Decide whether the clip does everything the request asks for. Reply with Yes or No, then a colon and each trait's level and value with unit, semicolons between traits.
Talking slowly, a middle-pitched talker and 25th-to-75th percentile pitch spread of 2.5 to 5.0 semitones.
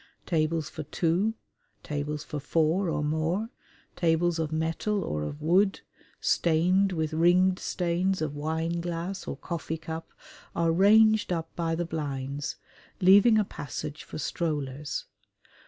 Yes: slow, 130 wpm; medium, 165 Hz; average, 2.9 semitones